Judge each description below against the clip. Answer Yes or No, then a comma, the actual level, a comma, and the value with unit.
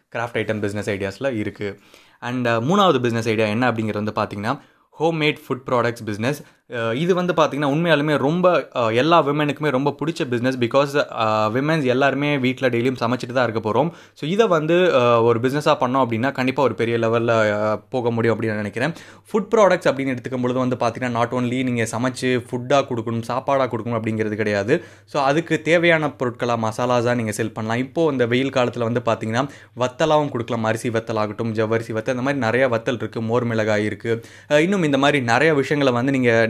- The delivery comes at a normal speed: No, fast, 170 wpm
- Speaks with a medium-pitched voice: No, low, 125 Hz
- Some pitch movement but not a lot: Yes, average, 3.7 semitones